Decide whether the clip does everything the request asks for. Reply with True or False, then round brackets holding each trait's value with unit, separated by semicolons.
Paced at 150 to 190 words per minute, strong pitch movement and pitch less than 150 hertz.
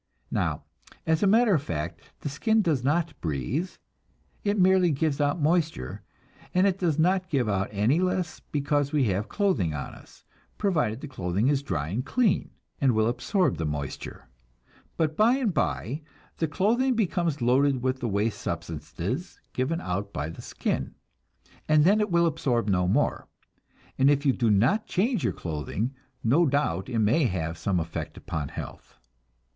True (165 wpm; 8.7 semitones; 140 Hz)